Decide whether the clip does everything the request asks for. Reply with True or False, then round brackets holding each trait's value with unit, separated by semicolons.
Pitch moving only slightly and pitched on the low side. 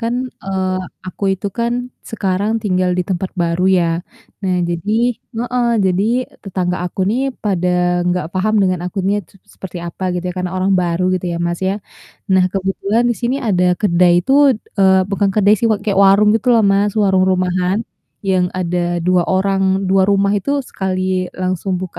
False (1.8 semitones; 190 Hz)